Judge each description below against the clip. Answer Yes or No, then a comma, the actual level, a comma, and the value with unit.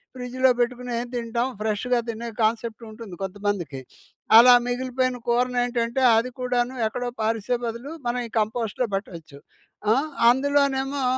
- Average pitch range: No, narrow, 2.2 semitones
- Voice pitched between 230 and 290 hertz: Yes, high, 240 Hz